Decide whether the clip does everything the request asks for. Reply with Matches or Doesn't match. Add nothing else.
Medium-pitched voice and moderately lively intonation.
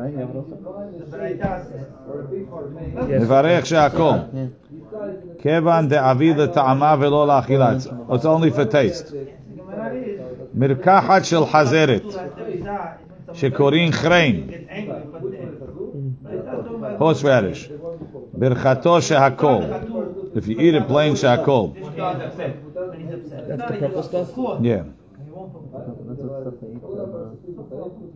Matches